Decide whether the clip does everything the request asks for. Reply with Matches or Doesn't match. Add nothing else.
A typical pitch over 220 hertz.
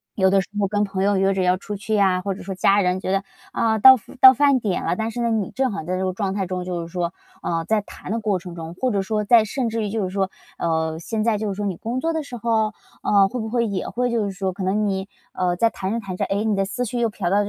Doesn't match